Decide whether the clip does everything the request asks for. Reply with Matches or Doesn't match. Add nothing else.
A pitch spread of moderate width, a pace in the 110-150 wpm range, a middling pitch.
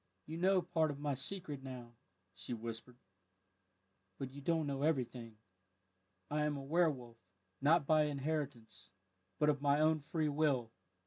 Matches